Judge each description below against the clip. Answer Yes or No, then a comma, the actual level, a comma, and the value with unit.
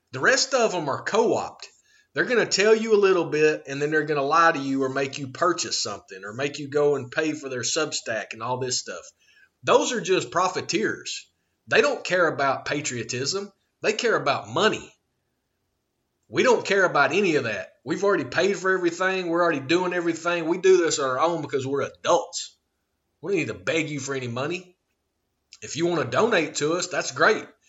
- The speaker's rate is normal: No, fast, 210 wpm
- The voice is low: No, medium, 165 Hz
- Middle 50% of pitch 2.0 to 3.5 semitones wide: No, average, 4.8 semitones